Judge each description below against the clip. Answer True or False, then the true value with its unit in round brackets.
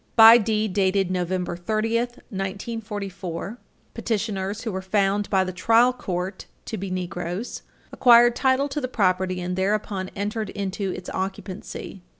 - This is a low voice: False (200 Hz)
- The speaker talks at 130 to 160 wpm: True (140 wpm)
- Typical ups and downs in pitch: True (3.2 semitones)